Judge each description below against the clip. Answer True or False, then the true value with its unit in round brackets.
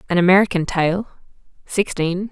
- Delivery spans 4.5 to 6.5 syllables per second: True (5.2 syllables/s)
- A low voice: False (185 Hz)